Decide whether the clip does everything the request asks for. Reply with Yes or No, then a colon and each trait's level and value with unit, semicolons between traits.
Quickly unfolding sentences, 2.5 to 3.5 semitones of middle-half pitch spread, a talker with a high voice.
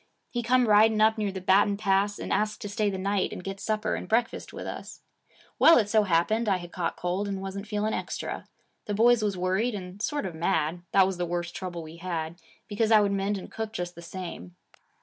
Yes: fast, 230 wpm; average, 3.0 semitones; high, 200 Hz